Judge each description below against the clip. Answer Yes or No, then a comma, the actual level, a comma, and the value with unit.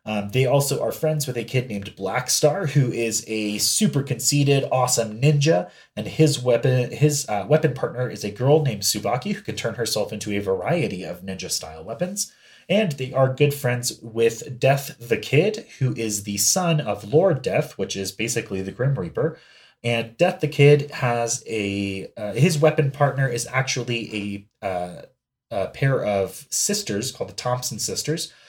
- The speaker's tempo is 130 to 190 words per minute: Yes, average, 175 wpm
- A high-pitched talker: No, low, 125 Hz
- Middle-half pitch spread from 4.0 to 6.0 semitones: Yes, wide, 5.6 semitones